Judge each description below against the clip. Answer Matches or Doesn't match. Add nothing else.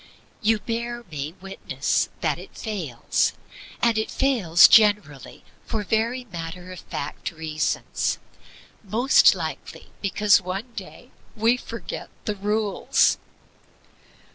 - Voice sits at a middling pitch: Doesn't match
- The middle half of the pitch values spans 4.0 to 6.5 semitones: Matches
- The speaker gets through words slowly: Matches